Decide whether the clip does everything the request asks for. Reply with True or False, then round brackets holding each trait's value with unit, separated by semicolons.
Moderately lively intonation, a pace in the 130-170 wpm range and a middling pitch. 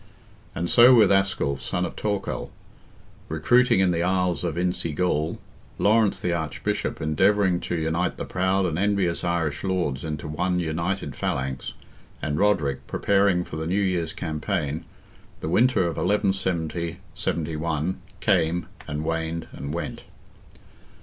False (3.4 semitones; 135 wpm; 85 Hz)